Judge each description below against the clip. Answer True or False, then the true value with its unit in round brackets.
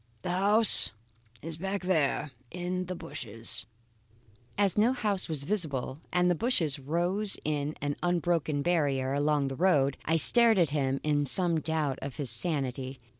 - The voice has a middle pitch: True (160 Hz)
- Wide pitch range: False (4.5 semitones)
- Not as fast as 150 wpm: False (155 wpm)